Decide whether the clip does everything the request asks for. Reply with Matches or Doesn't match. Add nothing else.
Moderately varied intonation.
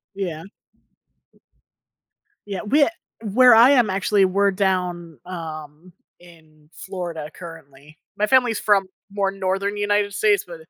Matches